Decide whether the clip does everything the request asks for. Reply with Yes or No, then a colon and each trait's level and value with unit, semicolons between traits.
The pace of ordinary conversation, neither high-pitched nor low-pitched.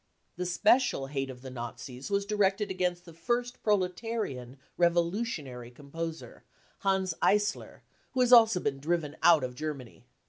Yes: average, 145 wpm; medium, 175 Hz